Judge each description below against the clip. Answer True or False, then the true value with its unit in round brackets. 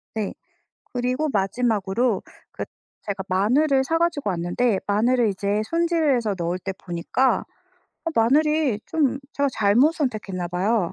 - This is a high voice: True (230 Hz)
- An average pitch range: False (6.0 semitones)